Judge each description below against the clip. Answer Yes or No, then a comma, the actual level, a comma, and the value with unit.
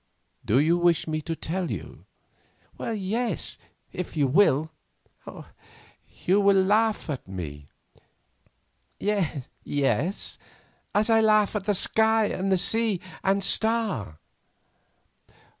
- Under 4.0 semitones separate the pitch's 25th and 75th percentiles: No, wide, 5.4 semitones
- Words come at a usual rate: No, slow, 100 wpm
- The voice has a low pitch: No, high, 190 Hz